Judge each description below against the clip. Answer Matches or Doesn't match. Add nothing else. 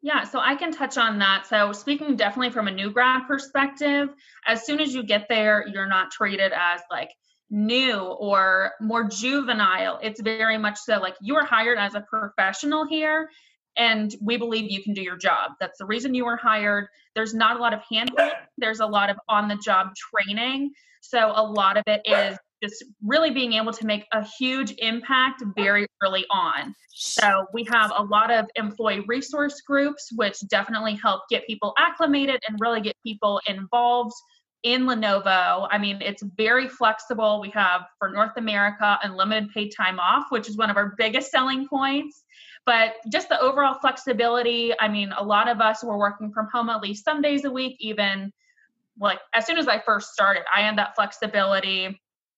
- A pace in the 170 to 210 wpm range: Matches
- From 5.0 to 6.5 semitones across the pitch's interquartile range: Doesn't match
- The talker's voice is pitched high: Matches